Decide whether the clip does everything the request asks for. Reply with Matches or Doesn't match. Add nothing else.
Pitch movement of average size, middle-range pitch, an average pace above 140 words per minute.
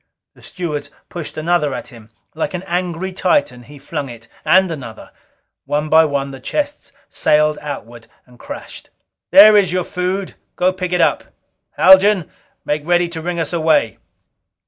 Matches